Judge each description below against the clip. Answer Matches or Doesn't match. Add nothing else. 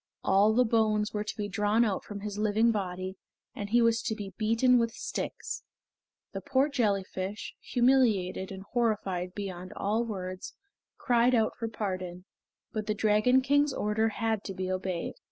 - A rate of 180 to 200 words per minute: Doesn't match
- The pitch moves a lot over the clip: Doesn't match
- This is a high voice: Matches